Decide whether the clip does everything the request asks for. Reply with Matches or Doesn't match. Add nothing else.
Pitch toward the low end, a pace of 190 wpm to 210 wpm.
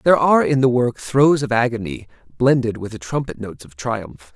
Matches